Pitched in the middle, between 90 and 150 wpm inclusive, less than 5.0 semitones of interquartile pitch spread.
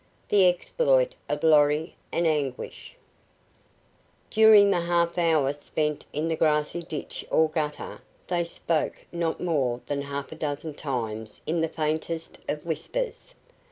Yes: medium, 160 Hz; average, 140 wpm; average, 2.7 semitones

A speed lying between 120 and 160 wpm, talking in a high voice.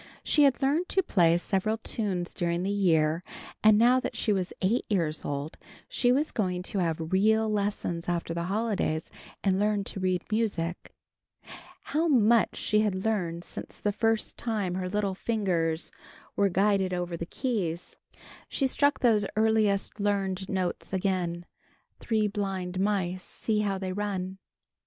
Yes: average, 155 wpm; high, 195 Hz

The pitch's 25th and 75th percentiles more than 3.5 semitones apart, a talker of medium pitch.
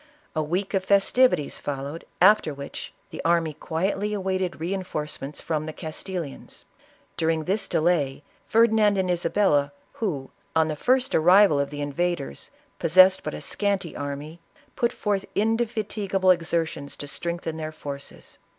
Yes: average, 4.4 semitones; medium, 170 Hz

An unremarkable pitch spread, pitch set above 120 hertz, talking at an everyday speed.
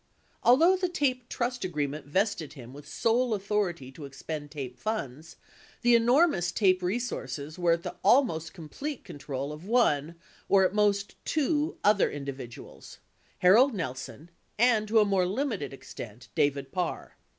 No: wide, 8.3 semitones; medium, 185 Hz; average, 150 wpm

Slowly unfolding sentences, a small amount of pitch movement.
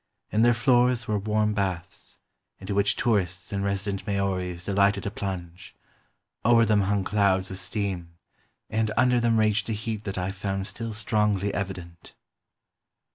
No: average, 150 wpm; narrow, 2.2 semitones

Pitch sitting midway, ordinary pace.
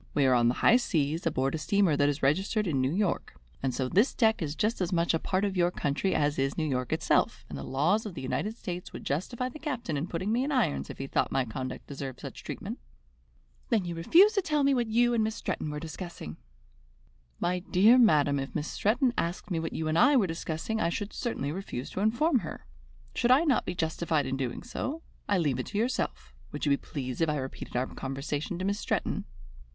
No: medium, 170 Hz; fast, 235 wpm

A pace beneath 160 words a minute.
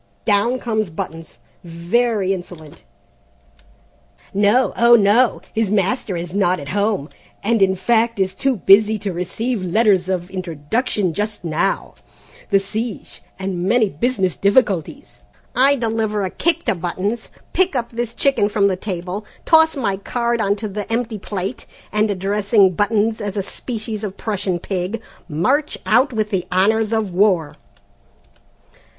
Yes: average, 145 wpm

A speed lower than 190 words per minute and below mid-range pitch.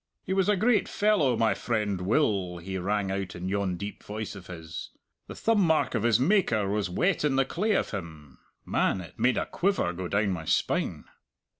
No: average, 200 wpm; low, 105 Hz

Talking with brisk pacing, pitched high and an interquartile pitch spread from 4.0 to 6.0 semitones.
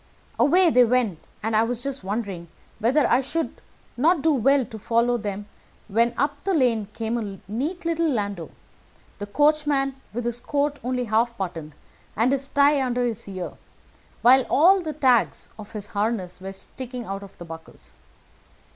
No: average, 170 wpm; high, 240 Hz; average, 5.2 semitones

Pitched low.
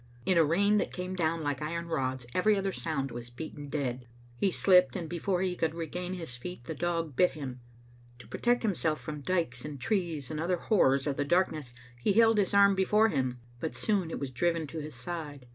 No: medium, 165 Hz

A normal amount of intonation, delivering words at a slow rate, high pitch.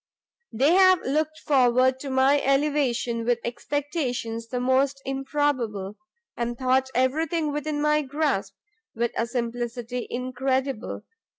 Yes: average, 3.2 semitones; slow, 115 wpm; very high, 260 Hz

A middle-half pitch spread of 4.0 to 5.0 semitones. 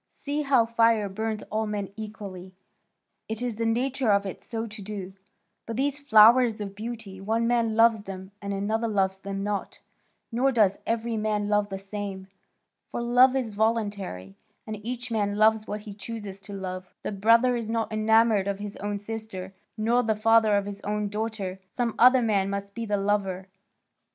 No: narrow, 2.4 semitones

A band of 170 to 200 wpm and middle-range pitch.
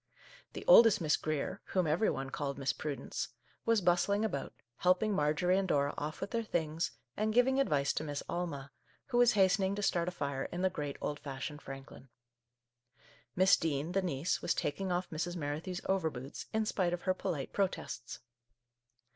Yes: average, 180 wpm; medium, 175 Hz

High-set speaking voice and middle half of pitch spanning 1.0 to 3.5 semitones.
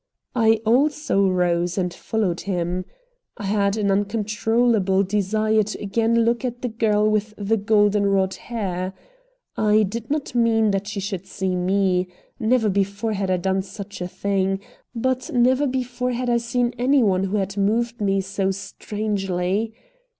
Yes: high, 205 Hz; average, 3.0 semitones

